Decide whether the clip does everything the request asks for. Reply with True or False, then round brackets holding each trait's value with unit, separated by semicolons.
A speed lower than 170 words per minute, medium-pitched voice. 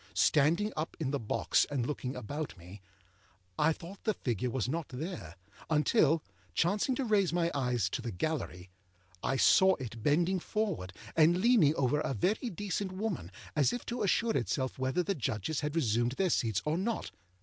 False (175 wpm; 155 Hz)